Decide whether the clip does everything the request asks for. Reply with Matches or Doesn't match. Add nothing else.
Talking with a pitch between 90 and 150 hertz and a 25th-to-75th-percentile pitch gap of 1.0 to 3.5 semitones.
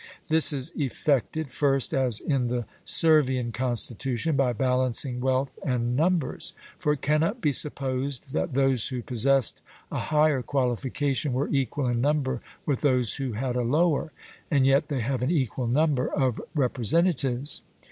Matches